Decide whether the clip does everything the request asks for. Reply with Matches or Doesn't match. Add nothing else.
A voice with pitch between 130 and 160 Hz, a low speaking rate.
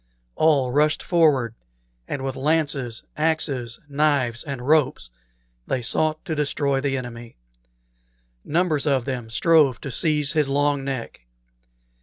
Matches